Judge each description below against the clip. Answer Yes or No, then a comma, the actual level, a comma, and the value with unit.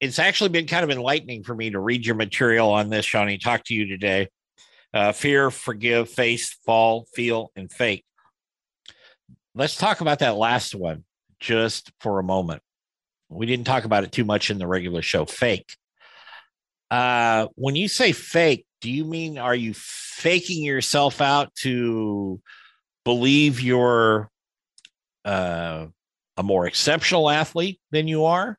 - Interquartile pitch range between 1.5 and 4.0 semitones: No, wide, 5.4 semitones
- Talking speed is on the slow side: No, average, 155 wpm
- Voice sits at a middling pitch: No, low, 120 Hz